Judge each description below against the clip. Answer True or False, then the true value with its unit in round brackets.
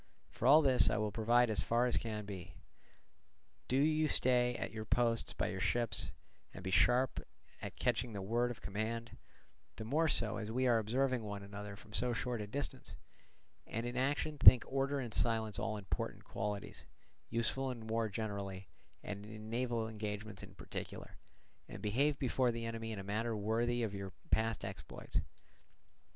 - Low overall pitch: True (115 Hz)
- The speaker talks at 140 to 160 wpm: False (170 wpm)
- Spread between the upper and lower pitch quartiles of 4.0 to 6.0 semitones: False (2.8 semitones)